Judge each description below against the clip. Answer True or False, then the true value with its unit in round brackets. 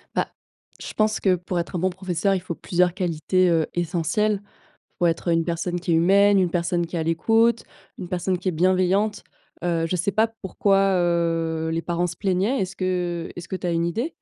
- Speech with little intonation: True (2.2 semitones)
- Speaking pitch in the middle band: True (180 Hz)